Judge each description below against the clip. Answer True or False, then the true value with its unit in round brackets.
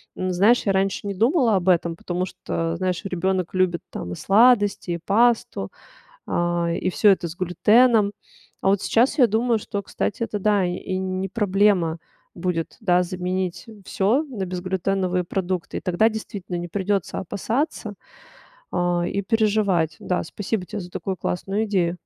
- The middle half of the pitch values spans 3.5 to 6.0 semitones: False (2.8 semitones)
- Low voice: False (190 Hz)